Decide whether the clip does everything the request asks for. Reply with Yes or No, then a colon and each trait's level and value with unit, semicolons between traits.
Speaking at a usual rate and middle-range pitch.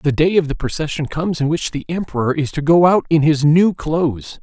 No: fast, 245 wpm; medium, 155 Hz